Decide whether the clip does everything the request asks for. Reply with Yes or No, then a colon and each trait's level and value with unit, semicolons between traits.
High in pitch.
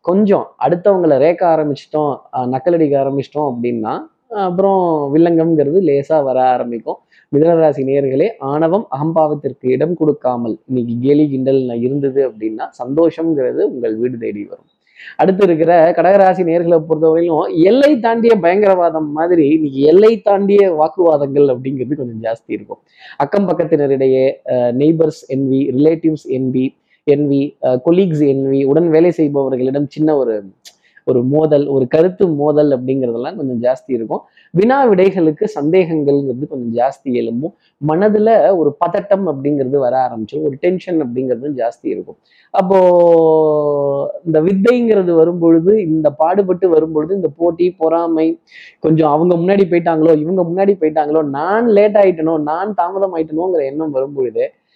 No: medium, 155 Hz